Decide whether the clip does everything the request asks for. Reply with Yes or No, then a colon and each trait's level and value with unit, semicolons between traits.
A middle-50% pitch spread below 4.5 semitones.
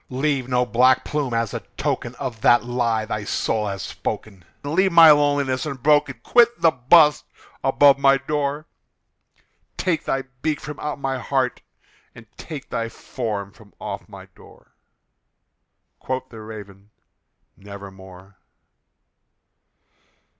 No: average, 5.1 semitones